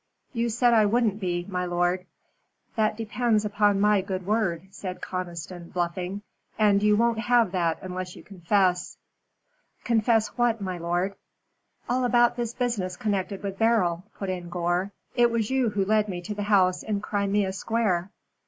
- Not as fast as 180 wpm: Yes, average, 160 wpm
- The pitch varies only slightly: No, average, 3.5 semitones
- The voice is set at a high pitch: Yes, high, 200 Hz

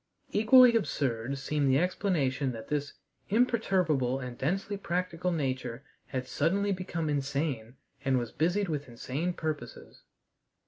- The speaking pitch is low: No, medium, 150 Hz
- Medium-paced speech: No, slow, 125 wpm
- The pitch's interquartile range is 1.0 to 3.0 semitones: No, wide, 5.6 semitones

